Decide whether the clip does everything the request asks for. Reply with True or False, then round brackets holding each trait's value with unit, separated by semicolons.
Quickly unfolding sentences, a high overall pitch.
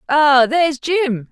False (135 wpm; 285 Hz)